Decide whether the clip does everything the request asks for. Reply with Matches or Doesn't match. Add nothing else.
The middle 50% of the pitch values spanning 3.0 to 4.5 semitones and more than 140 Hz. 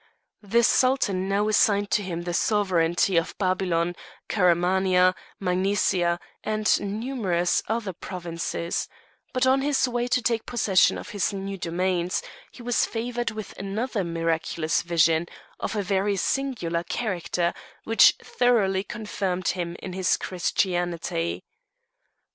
Matches